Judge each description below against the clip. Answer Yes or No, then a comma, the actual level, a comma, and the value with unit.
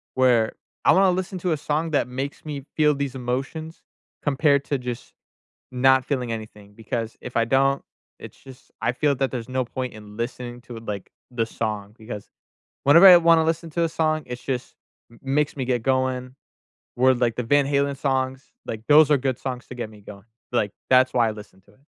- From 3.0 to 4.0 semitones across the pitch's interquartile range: Yes, average, 3.4 semitones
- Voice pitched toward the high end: No, low, 130 Hz